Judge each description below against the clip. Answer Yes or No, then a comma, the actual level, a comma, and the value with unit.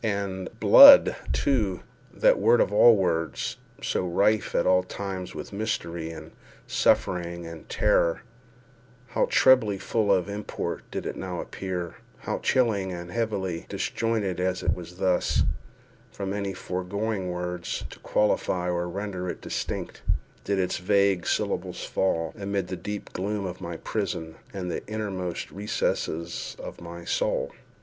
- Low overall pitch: Yes, very low, 95 Hz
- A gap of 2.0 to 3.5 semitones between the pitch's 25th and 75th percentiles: Yes, average, 2.9 semitones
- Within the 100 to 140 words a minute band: Yes, slow, 135 wpm